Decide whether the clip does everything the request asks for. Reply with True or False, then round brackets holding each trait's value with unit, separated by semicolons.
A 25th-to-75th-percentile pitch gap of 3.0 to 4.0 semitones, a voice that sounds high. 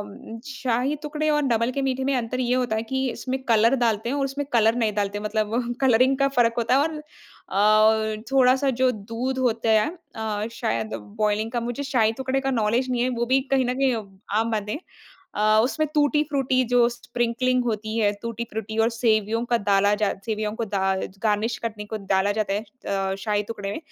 True (3.3 semitones; 230 Hz)